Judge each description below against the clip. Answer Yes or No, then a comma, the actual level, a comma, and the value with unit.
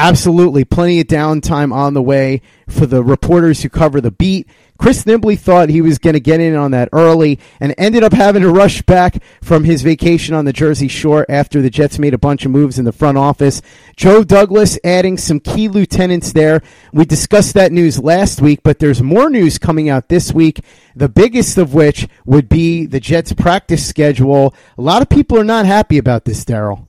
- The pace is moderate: No, fast, 210 wpm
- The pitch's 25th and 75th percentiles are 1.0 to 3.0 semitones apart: No, average, 3.8 semitones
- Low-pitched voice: No, medium, 155 Hz